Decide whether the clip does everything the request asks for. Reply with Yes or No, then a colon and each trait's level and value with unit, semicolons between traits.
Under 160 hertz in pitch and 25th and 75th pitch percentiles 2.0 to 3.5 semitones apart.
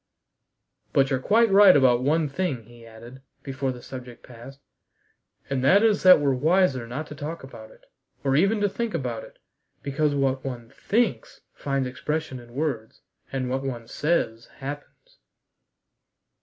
No: low, 135 Hz; average, 4.1 semitones